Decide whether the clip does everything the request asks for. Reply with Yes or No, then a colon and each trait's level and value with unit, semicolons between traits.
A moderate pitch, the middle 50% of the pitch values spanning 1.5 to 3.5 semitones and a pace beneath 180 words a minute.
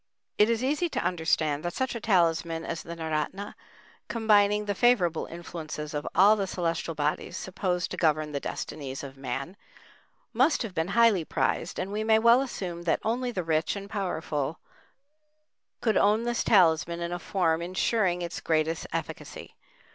No: medium, 175 Hz; average, 4.5 semitones; average, 165 wpm